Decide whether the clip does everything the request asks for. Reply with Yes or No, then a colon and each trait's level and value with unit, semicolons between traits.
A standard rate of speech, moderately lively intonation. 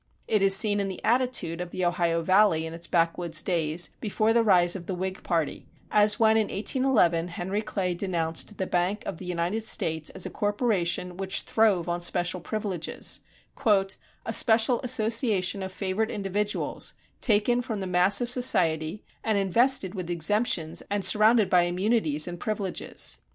Yes: average, 165 wpm; average, 3.7 semitones